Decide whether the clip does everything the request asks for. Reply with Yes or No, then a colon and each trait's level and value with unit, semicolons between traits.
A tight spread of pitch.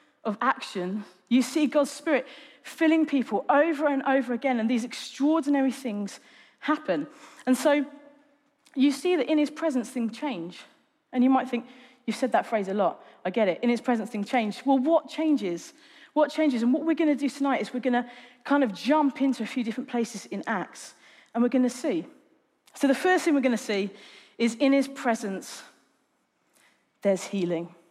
No: average, 3.8 semitones